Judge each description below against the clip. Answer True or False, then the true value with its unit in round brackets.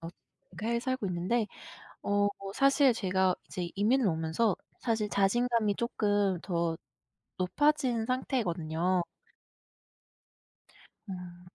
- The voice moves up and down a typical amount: True (4.7 semitones)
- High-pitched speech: True (205 Hz)